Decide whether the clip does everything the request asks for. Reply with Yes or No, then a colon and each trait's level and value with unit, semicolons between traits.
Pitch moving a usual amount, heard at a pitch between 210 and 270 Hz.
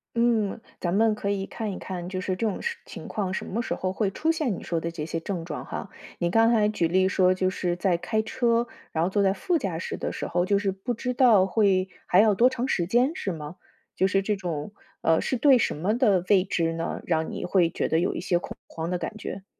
No: average, 3.9 semitones; high, 195 Hz